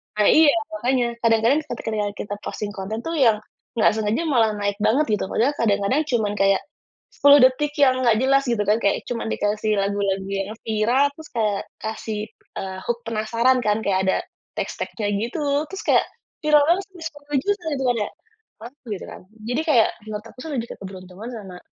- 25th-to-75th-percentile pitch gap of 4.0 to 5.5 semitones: Yes, average, 4.6 semitones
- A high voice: Yes, high, 230 Hz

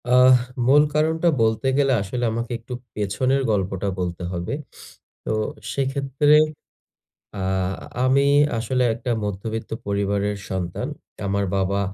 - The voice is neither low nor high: No, low, 115 Hz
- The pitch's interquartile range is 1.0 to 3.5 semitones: No, average, 5.1 semitones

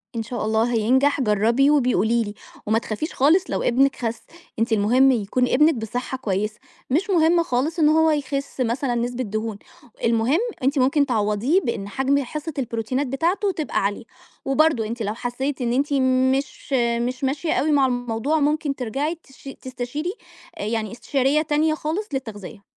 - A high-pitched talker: Yes, very high, 255 Hz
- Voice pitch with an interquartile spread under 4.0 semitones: No, average, 4.4 semitones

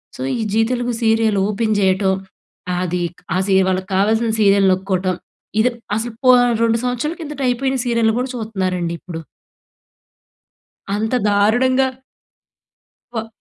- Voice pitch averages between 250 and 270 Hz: No, high, 220 Hz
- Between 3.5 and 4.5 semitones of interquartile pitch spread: Yes, average, 4.1 semitones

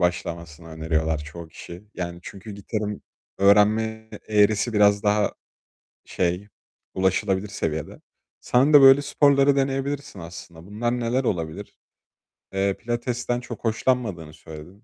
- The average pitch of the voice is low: Yes, low, 105 Hz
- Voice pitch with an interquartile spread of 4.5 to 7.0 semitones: Yes, wide, 5.5 semitones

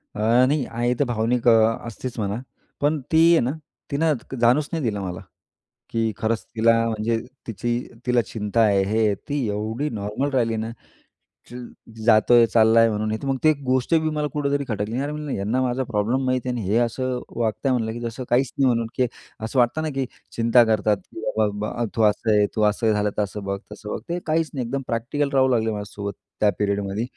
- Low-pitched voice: Yes, low, 115 Hz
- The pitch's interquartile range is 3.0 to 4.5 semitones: Yes, average, 3.4 semitones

